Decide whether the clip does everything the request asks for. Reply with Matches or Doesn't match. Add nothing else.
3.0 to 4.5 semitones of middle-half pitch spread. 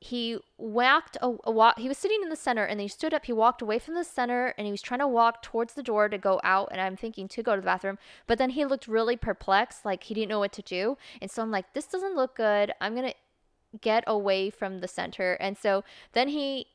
Matches